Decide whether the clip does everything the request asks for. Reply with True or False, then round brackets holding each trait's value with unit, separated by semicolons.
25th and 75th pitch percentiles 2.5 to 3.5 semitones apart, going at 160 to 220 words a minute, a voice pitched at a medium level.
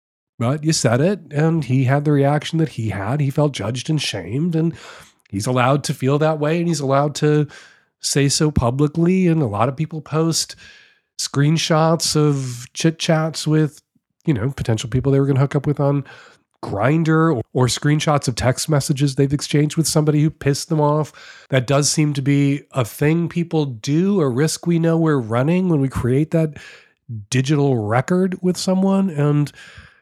True (2.9 semitones; 185 wpm; 150 Hz)